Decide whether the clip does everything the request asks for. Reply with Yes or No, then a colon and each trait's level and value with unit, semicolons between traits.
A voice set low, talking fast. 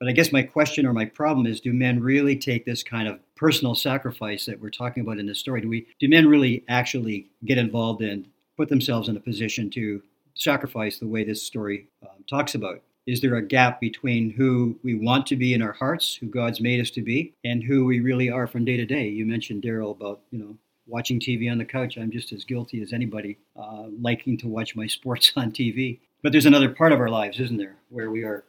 Yes: low, 120 Hz; fast, 240 wpm